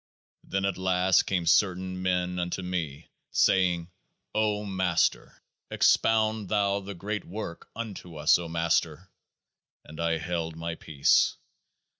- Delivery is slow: Yes, slow, 125 wpm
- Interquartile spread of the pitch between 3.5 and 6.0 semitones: No, average, 2.7 semitones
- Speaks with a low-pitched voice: Yes, very low, 90 Hz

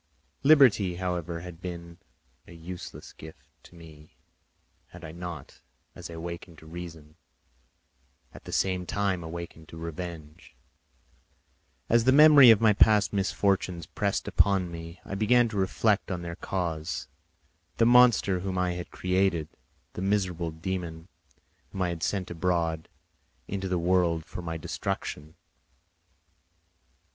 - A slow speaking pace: Yes, slow, 130 wpm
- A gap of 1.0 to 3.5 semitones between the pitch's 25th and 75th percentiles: Yes, average, 2.7 semitones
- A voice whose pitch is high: No, very low, 90 Hz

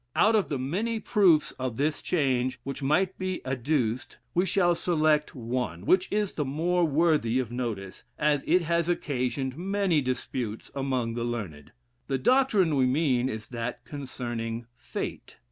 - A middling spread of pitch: No, wide, 5.8 semitones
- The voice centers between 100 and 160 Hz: Yes, medium, 140 Hz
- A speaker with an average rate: Yes, average, 155 wpm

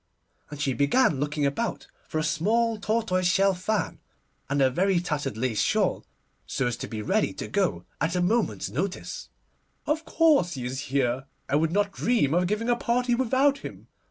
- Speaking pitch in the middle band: Yes, medium, 180 Hz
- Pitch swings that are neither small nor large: No, wide, 8.0 semitones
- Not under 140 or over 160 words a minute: No, average, 185 wpm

